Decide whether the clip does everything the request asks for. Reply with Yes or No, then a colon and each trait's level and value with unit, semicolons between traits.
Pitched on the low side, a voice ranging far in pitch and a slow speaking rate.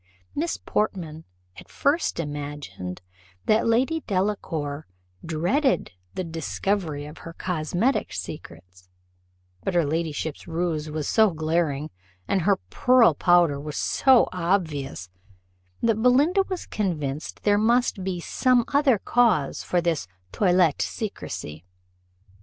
No: medium, 175 Hz; wide, 6.3 semitones; slow, 115 wpm